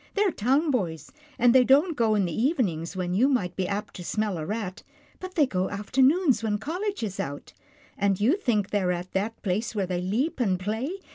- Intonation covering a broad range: Yes, wide, 6.1 semitones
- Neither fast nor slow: No, fast, 220 wpm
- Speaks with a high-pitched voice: Yes, high, 215 Hz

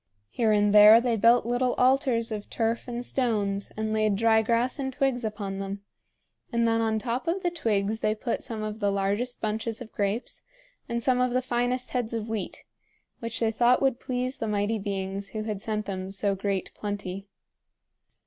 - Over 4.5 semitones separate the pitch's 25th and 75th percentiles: No, average, 2.9 semitones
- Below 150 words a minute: No, average, 190 wpm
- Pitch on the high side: Yes, high, 225 Hz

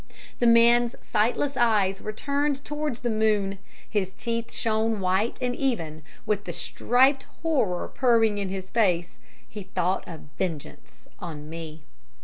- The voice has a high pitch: Yes, high, 215 Hz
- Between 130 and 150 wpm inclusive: Yes, average, 140 wpm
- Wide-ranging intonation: No, average, 4.2 semitones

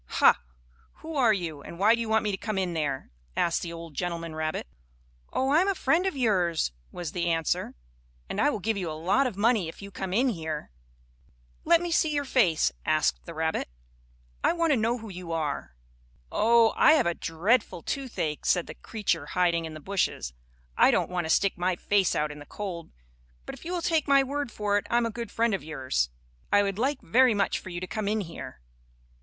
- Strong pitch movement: Yes, wide, 6.1 semitones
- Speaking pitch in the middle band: No, high, 195 Hz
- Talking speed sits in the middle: No, fast, 225 wpm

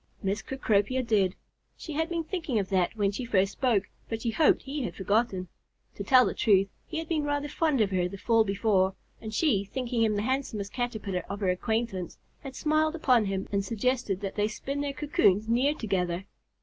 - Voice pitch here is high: Yes, high, 220 Hz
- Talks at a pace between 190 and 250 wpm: Yes, average, 200 wpm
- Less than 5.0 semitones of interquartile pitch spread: No, average, 5.3 semitones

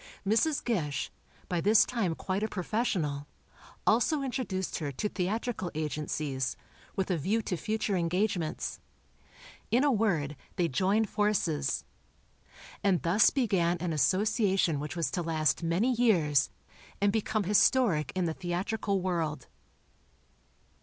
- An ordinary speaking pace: No, slow, 125 wpm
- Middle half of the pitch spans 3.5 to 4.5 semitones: No, average, 5.1 semitones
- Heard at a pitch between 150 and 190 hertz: Yes, medium, 185 Hz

